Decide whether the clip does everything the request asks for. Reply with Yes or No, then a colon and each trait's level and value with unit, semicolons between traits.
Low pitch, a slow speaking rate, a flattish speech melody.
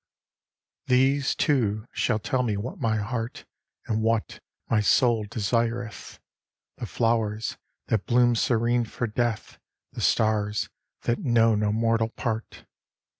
Yes: low, 115 Hz; slow, 125 wpm; narrow, 1.8 semitones